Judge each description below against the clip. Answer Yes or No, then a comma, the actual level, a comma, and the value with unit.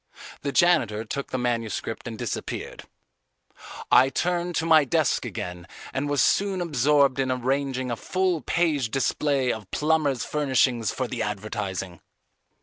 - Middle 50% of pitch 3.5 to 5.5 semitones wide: Yes, average, 4.5 semitones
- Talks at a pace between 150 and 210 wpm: No, average, 140 wpm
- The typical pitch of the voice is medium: No, low, 130 Hz